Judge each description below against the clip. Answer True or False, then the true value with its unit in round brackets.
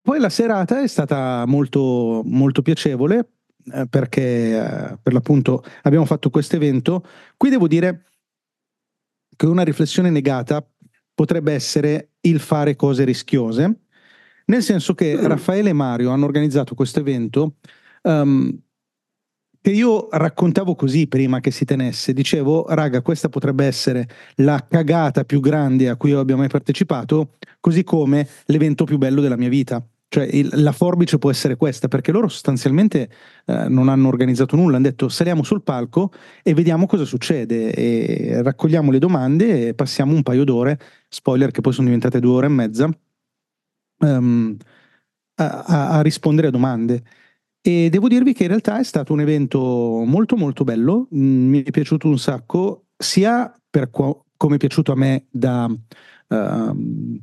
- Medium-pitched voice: True (145 Hz)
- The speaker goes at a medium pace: True (155 wpm)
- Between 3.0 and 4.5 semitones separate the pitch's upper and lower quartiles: True (4.0 semitones)